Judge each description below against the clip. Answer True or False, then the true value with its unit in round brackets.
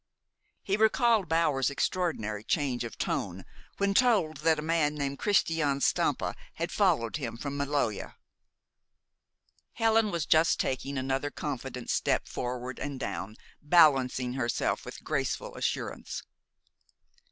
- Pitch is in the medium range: True (145 Hz)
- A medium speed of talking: False (120 wpm)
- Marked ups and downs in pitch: False (4.6 semitones)